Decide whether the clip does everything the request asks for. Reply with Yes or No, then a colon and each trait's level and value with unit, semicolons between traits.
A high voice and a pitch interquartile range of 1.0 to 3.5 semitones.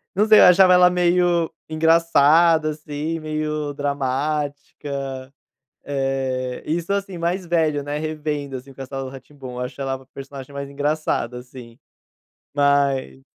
No: medium, 145 Hz; average, 3.2 semitones